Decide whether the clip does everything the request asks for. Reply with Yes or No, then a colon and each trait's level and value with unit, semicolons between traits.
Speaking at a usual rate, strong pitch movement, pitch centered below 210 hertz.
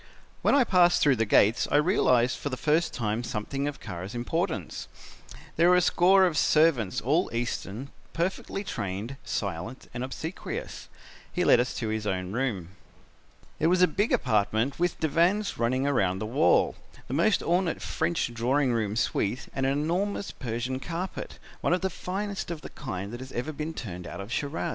Yes: average, 180 wpm; wide, 7.0 semitones; low, 135 Hz